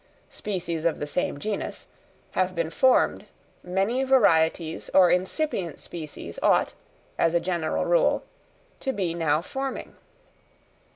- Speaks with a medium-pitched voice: Yes, medium, 180 Hz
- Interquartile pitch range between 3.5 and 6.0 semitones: Yes, average, 4.4 semitones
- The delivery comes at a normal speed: No, slow, 125 wpm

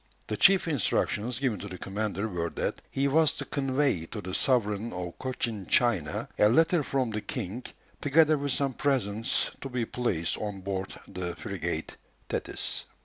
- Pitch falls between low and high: No, low, 110 Hz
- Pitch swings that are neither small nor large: No, wide, 5.8 semitones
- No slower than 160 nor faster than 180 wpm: Yes, average, 170 wpm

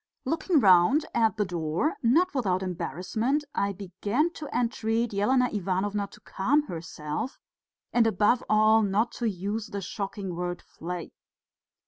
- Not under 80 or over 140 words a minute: Yes, slow, 135 wpm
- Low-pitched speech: No, high, 210 Hz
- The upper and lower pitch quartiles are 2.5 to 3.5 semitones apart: No, average, 4.6 semitones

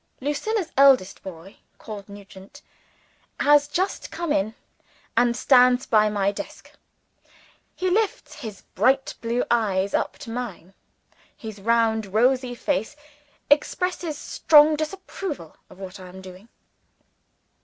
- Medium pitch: No, high, 235 Hz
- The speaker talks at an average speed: No, slow, 120 wpm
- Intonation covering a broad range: Yes, wide, 6.5 semitones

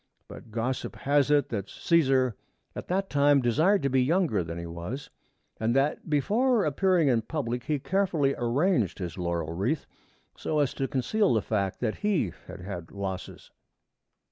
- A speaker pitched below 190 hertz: Yes, low, 135 Hz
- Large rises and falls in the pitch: Yes, wide, 6.8 semitones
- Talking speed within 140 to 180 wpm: Yes, average, 165 wpm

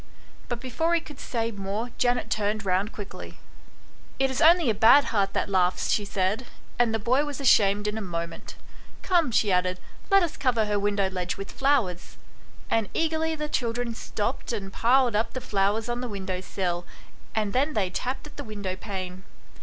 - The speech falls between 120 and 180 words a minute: No, average, 195 wpm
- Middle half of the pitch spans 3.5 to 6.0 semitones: Yes, average, 4.7 semitones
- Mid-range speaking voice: No, high, 220 Hz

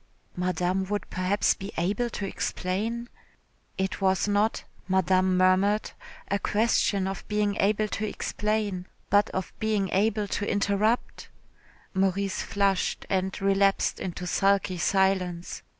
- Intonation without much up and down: Yes, narrow, 1.7 semitones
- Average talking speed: No, slow, 120 wpm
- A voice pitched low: No, high, 195 Hz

